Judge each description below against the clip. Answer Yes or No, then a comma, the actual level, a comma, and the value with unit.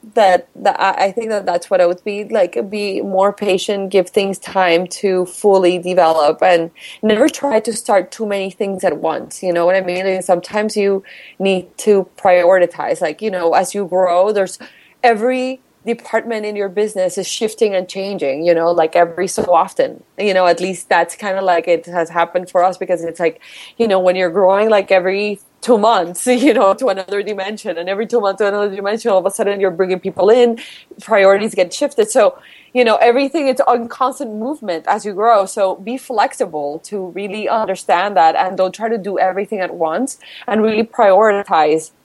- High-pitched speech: Yes, high, 195 Hz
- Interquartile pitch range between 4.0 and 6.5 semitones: No, average, 3.2 semitones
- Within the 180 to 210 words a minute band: Yes, average, 200 wpm